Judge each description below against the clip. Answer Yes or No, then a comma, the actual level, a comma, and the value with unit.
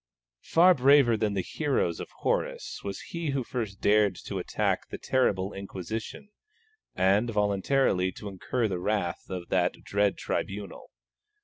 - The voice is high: No, low, 105 Hz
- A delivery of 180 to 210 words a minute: No, average, 140 wpm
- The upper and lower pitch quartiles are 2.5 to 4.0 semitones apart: No, average, 4.7 semitones